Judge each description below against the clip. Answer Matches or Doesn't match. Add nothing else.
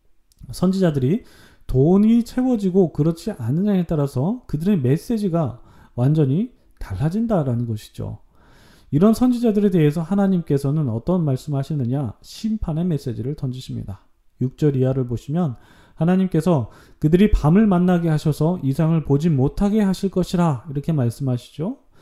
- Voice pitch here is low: Doesn't match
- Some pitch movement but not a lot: Doesn't match